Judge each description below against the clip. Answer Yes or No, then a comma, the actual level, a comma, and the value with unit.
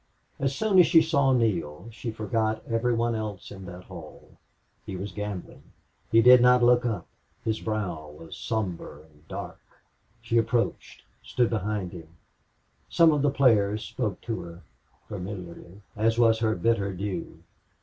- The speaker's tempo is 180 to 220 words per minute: No, average, 155 wpm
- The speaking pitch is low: Yes, low, 110 Hz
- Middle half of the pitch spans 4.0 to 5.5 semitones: Yes, average, 4.3 semitones